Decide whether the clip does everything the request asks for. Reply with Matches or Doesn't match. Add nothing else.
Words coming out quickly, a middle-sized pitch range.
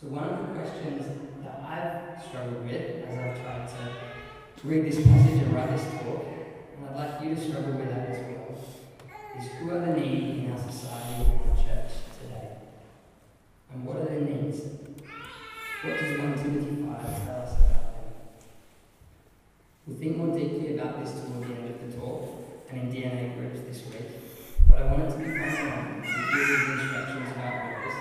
Doesn't match